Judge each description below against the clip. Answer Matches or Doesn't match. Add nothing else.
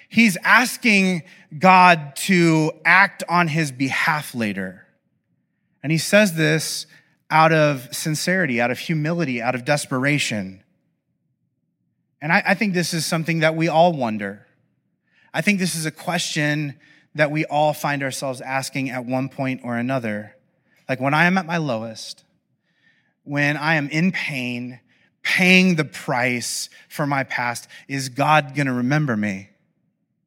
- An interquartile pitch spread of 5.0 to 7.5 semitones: Doesn't match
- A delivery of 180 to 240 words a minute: Doesn't match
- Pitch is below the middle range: Doesn't match